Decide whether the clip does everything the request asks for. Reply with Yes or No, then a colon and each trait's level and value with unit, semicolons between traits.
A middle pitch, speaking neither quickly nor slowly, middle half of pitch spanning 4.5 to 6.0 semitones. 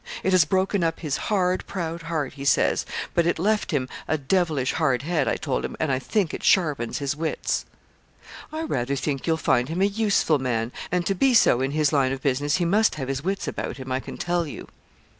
No: medium, 155 Hz; fast, 225 wpm; average, 5.1 semitones